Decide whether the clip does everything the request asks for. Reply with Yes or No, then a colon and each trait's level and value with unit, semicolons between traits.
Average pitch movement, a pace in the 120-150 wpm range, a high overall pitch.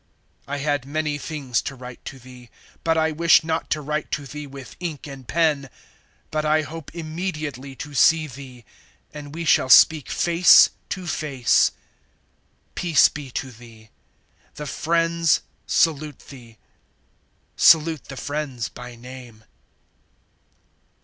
No: average, 3.3 semitones; slow, 135 wpm; medium, 145 Hz